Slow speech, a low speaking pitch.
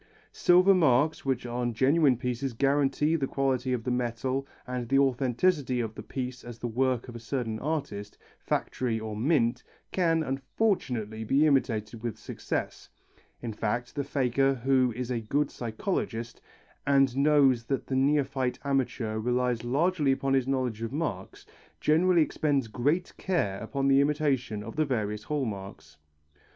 No: average, 155 wpm; low, 130 Hz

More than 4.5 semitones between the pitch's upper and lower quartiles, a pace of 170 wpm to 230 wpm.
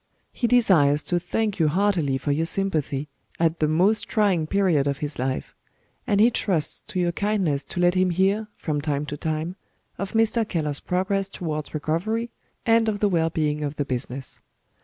Yes: average, 5.0 semitones; average, 180 wpm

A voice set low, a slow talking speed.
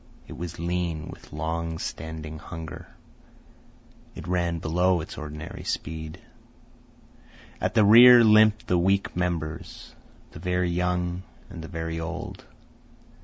Yes: very low, 85 Hz; slow, 120 wpm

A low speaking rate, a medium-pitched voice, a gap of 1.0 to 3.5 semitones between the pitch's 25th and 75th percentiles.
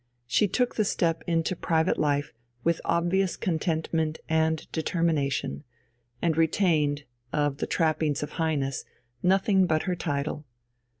Yes: slow, 125 wpm; medium, 160 Hz; narrow, 2.6 semitones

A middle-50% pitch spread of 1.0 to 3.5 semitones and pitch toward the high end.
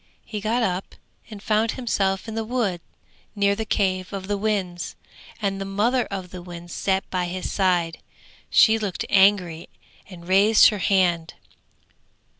Yes: average, 2.8 semitones; high, 195 Hz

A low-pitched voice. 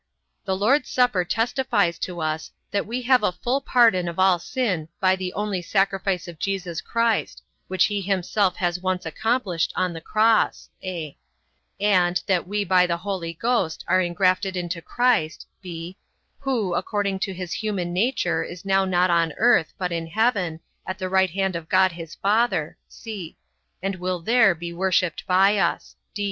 No: medium, 185 Hz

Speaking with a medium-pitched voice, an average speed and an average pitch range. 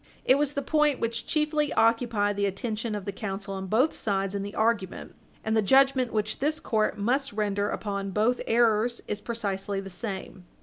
No: high, 215 Hz; average, 185 wpm; average, 3.5 semitones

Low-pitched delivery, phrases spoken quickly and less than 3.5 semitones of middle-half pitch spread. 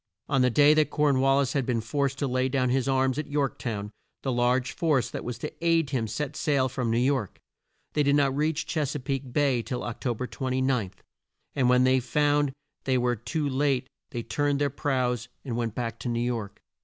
Yes: low, 130 Hz; fast, 220 wpm; narrow, 2.6 semitones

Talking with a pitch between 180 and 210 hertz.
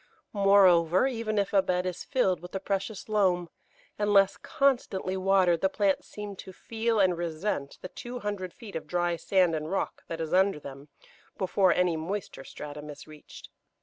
Yes: high, 190 Hz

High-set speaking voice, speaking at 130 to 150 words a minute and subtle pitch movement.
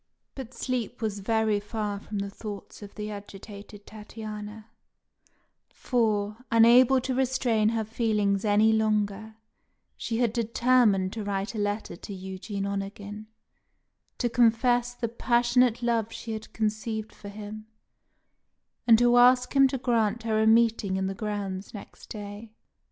Yes: high, 220 Hz; average, 140 wpm; narrow, 2.3 semitones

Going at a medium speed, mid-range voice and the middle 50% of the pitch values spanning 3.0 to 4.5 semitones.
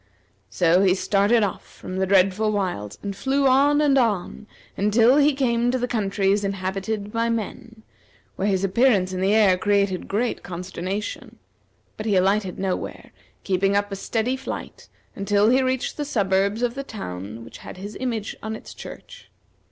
No: average, 165 wpm; high, 205 Hz; average, 3.6 semitones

